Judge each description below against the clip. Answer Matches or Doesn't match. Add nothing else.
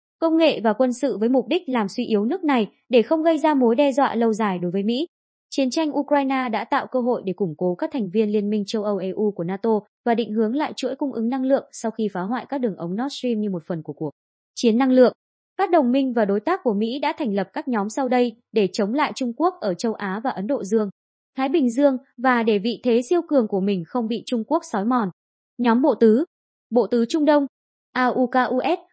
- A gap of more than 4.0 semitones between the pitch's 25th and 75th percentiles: Matches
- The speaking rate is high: Matches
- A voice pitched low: Doesn't match